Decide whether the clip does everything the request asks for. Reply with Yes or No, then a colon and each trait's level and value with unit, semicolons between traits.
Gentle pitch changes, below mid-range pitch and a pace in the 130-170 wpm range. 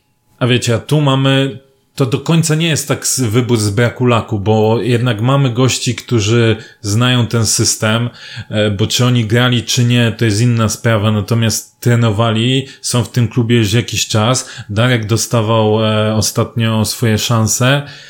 Yes: narrow, 2.2 semitones; low, 120 Hz; average, 155 wpm